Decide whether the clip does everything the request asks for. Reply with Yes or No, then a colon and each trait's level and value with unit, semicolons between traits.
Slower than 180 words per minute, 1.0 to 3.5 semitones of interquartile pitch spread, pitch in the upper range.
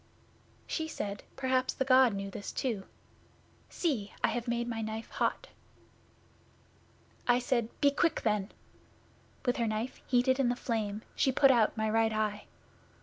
Yes: average, 150 wpm; average, 3.2 semitones; high, 235 Hz